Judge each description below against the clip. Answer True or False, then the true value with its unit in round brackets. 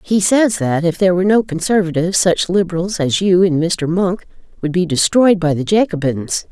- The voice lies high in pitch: False (180 Hz)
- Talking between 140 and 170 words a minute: False (195 wpm)